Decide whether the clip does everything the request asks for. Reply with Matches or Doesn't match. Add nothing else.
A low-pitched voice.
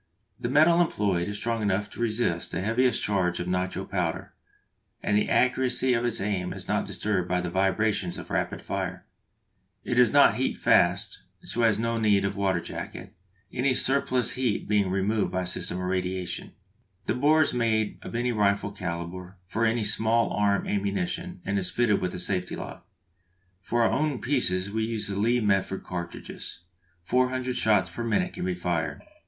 Matches